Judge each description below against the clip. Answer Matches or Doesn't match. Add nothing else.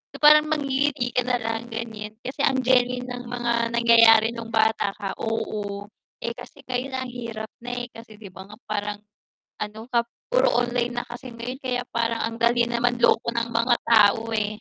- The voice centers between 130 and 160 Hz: Doesn't match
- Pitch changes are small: Matches